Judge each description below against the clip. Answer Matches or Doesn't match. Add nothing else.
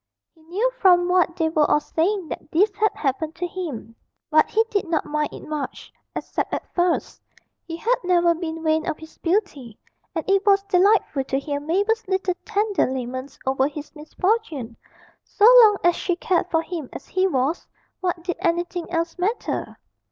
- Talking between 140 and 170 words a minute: Doesn't match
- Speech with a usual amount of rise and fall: Matches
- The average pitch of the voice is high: Matches